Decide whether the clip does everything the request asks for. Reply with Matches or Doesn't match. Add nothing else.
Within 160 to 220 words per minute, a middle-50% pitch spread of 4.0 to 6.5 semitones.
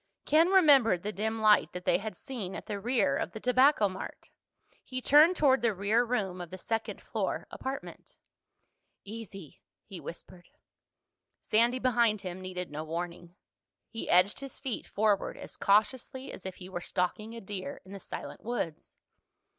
Matches